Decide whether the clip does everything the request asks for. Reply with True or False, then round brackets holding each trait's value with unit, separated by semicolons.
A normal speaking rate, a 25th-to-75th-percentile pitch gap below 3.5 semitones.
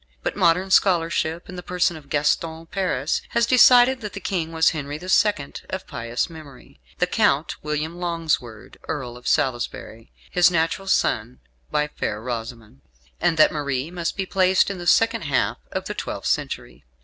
False (170 wpm; 4.7 semitones)